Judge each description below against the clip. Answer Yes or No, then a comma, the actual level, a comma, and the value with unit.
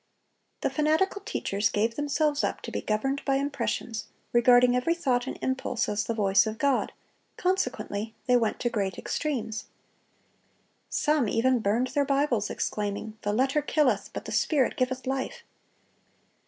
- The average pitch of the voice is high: Yes, very high, 250 Hz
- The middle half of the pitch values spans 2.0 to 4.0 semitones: No, average, 4.5 semitones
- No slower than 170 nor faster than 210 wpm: No, average, 155 wpm